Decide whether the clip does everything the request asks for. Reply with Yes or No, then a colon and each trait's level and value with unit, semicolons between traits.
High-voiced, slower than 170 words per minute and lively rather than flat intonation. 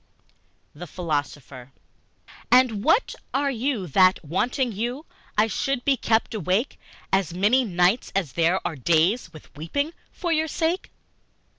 Yes: high, 205 Hz; slow, 135 wpm; wide, 7.3 semitones